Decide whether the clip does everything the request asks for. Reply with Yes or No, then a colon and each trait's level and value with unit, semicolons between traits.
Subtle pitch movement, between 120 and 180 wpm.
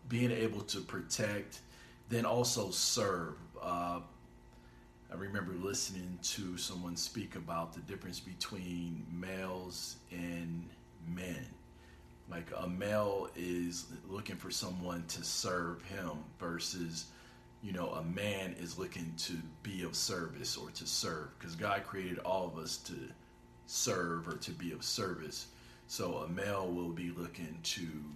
Yes: narrow, 1.9 semitones; average, 140 wpm